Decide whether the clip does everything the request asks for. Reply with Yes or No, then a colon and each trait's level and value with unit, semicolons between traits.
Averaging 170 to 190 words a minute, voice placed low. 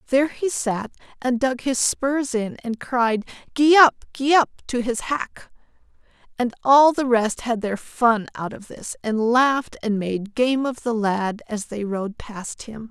No: average, 185 wpm; high, 240 Hz